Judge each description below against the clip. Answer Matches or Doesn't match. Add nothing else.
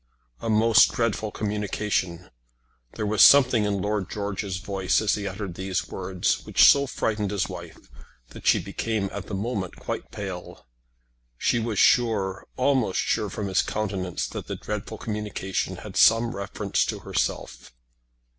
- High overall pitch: Doesn't match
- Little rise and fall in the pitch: Matches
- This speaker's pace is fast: Doesn't match